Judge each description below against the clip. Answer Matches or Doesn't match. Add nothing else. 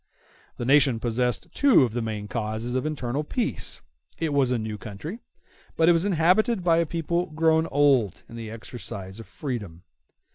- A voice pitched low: Matches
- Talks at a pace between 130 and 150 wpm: Doesn't match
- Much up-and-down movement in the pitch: Matches